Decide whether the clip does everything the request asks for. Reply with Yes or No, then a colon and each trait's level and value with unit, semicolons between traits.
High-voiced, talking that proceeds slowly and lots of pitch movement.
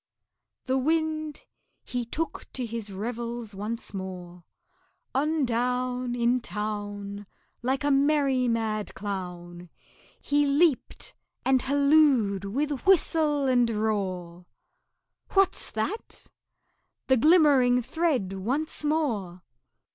Yes: high, 245 Hz; slow, 100 wpm; wide, 5.9 semitones